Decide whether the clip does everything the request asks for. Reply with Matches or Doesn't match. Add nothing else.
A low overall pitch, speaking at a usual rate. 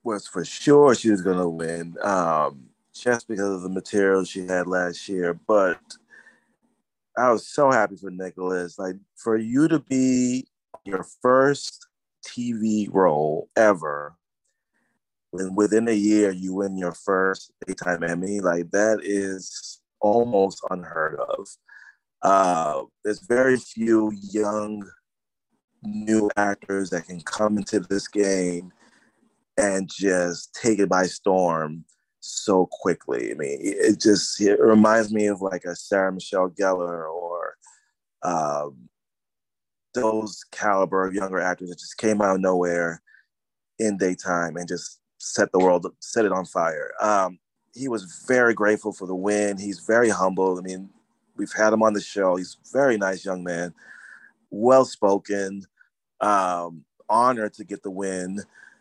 Matches